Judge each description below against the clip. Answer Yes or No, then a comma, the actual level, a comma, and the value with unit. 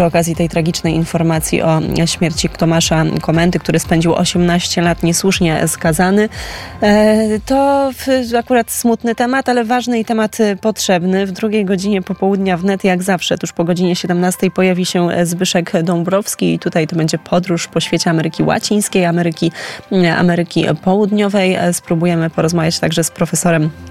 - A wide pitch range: No, average, 3.2 semitones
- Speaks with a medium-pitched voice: Yes, medium, 175 Hz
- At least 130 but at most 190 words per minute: Yes, average, 140 wpm